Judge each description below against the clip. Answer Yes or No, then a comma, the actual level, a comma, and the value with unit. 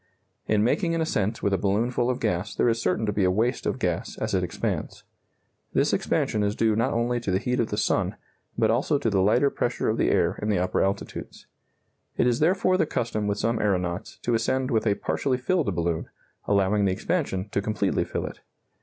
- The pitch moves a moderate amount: Yes, average, 3.6 semitones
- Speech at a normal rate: No, fast, 220 wpm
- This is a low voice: Yes, low, 110 Hz